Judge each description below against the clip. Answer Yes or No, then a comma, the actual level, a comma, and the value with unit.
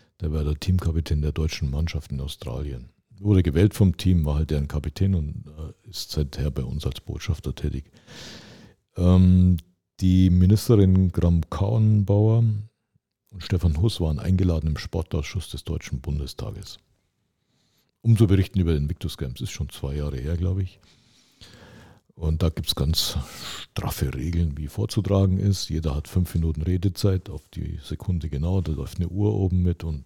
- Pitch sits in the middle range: No, very low, 90 Hz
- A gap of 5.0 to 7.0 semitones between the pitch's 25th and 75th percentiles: No, average, 4.1 semitones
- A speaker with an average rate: Yes, average, 160 wpm